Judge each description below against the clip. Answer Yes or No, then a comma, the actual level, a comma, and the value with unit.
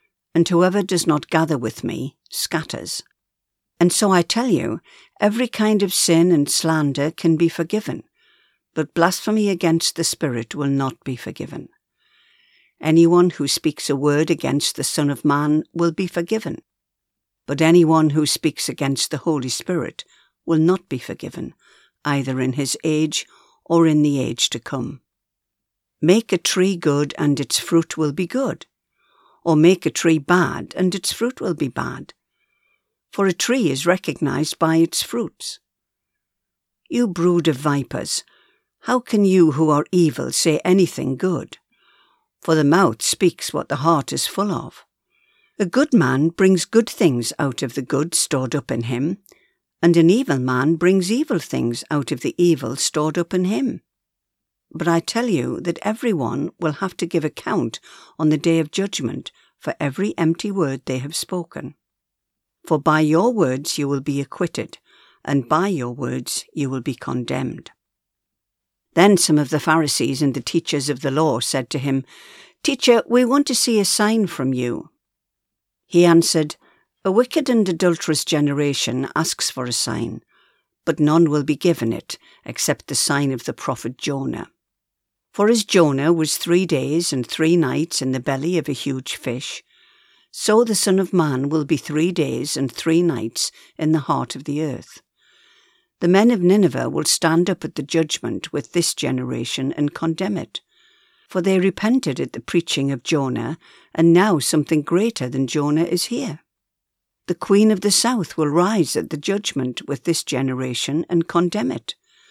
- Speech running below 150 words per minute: No, average, 170 wpm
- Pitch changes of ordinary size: Yes, average, 4.6 semitones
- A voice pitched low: No, medium, 160 Hz